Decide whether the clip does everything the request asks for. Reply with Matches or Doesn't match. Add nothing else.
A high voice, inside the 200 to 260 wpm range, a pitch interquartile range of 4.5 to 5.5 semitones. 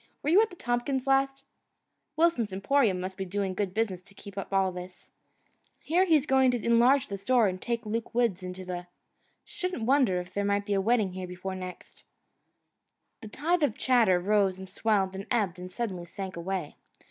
Matches